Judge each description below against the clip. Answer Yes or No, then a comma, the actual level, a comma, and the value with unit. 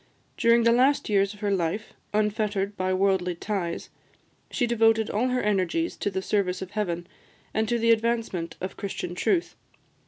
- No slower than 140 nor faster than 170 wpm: Yes, average, 165 wpm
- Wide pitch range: No, average, 3.4 semitones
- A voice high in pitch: Yes, high, 205 Hz